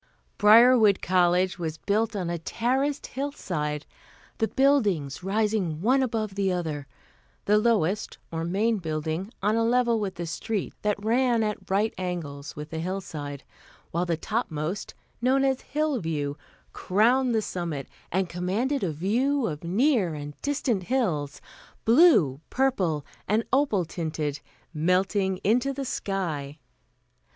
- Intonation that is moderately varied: No, wide, 6.1 semitones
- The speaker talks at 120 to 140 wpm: Yes, slow, 135 wpm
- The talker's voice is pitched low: No, high, 195 Hz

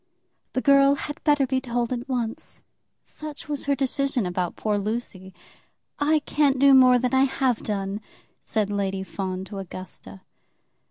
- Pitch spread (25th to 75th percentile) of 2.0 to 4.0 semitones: No, wide, 5.6 semitones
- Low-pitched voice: No, very high, 250 Hz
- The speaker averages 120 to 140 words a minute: No, average, 155 wpm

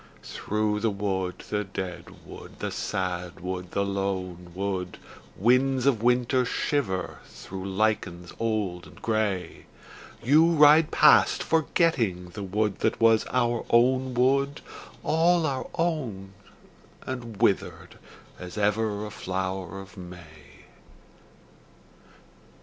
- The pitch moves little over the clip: No, average, 5.2 semitones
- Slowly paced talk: Yes, slow, 115 wpm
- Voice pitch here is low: Yes, low, 105 Hz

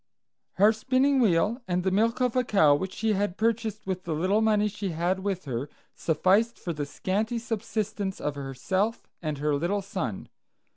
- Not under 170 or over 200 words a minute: Yes, average, 180 wpm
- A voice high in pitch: Yes, high, 195 Hz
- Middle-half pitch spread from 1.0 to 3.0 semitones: No, average, 4.6 semitones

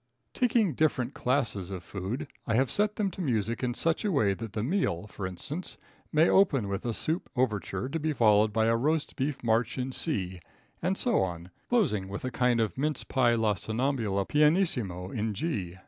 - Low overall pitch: Yes, low, 120 Hz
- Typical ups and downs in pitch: No, wide, 6.8 semitones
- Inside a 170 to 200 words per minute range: Yes, average, 195 wpm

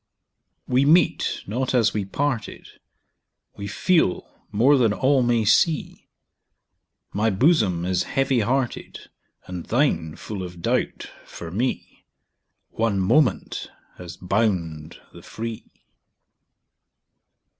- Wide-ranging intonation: Yes, wide, 6.0 semitones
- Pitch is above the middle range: No, low, 110 Hz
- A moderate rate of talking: No, slow, 105 wpm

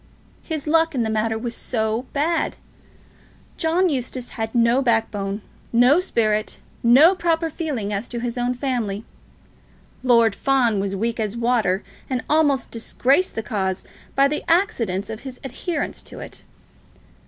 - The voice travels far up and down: No, average, 4.4 semitones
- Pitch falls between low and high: No, high, 240 Hz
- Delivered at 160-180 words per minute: No, average, 150 wpm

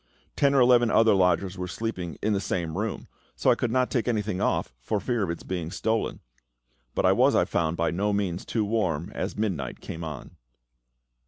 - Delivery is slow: No, average, 200 wpm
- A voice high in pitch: No, low, 100 Hz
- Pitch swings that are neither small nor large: Yes, average, 4.6 semitones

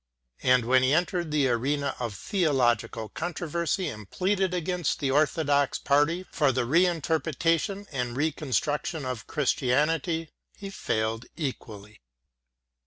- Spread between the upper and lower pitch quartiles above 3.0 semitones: Yes, average, 4.9 semitones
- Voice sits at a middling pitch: Yes, medium, 145 Hz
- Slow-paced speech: Yes, slow, 120 wpm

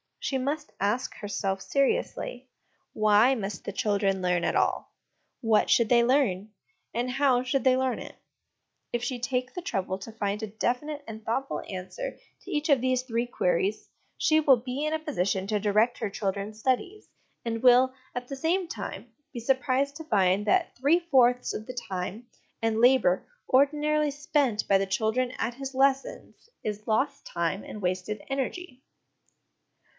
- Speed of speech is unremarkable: Yes, average, 165 wpm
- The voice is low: No, high, 245 Hz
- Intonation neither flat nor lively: Yes, average, 4.7 semitones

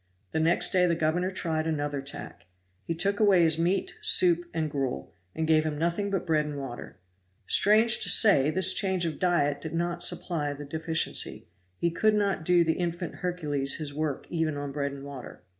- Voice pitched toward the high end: No, medium, 160 Hz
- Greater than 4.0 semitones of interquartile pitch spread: No, average, 3.4 semitones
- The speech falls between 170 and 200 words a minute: Yes, average, 190 wpm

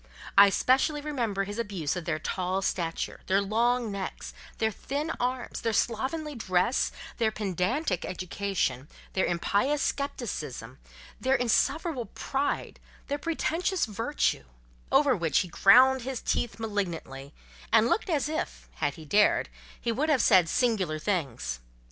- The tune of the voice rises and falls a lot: Yes, wide, 6.3 semitones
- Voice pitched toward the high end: Yes, high, 220 Hz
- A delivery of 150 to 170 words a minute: No, slow, 135 wpm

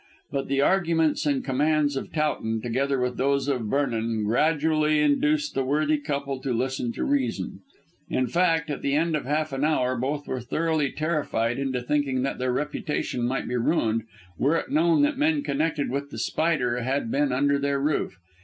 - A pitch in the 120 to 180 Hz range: Yes, medium, 140 Hz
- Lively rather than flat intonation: No, average, 3.2 semitones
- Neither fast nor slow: Yes, average, 180 wpm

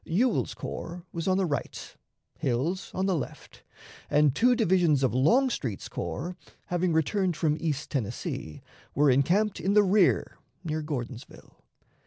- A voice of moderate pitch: Yes, medium, 165 Hz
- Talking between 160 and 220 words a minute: No, average, 140 wpm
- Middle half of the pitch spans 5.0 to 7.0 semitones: Yes, average, 5.3 semitones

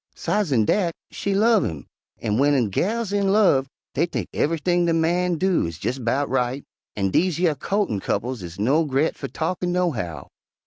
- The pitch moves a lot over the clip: Yes, wide, 6.7 semitones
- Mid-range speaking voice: Yes, medium, 155 Hz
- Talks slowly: No, average, 180 wpm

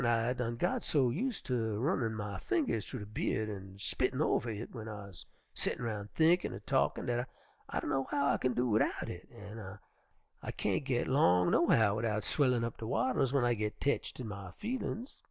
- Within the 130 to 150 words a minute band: No, average, 200 wpm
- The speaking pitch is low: Yes, low, 115 Hz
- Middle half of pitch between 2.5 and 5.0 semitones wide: Yes, average, 3.8 semitones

